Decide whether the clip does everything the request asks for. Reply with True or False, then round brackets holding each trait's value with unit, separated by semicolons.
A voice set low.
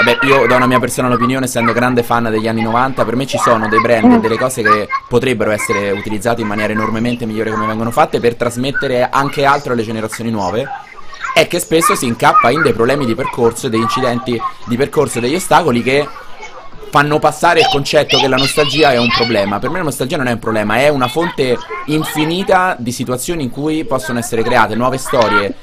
True (125 Hz)